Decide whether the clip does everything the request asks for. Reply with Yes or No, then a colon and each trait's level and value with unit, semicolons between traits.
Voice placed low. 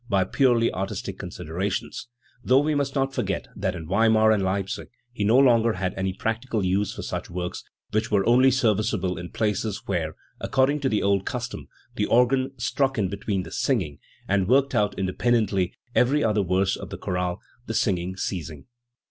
Yes: low, 105 Hz